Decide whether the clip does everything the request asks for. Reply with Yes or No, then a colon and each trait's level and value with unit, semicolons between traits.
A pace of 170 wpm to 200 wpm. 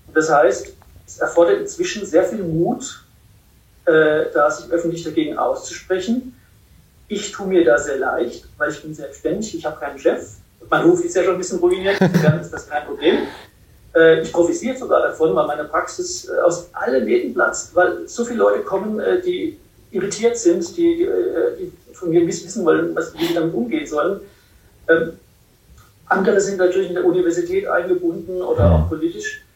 Yes: average, 180 wpm